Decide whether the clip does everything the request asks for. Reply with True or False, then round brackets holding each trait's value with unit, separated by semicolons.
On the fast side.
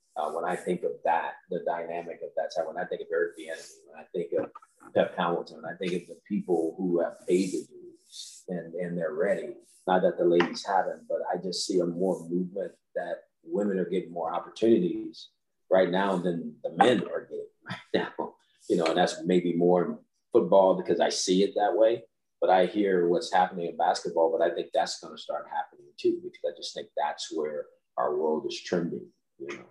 True (210 wpm)